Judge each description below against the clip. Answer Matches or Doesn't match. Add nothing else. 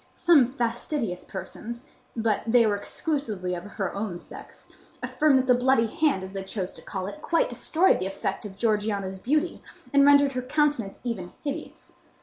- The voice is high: Matches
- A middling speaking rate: Matches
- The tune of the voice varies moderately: Doesn't match